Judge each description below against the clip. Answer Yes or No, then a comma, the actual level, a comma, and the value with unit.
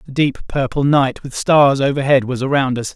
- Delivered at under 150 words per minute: No, fast, 205 wpm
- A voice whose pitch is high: No, low, 135 Hz